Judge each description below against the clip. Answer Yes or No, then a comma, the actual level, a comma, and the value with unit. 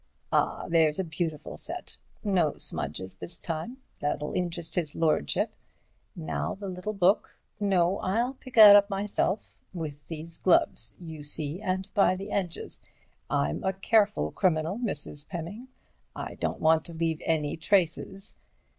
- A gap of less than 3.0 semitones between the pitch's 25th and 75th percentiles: No, average, 4.1 semitones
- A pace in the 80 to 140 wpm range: Yes, slow, 135 wpm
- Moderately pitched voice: Yes, medium, 175 Hz